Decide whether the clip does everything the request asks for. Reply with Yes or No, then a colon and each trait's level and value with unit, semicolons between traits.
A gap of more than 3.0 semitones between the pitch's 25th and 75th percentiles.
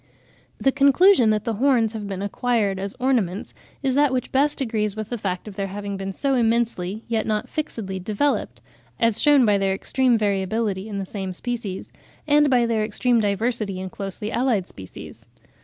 Yes: average, 4.0 semitones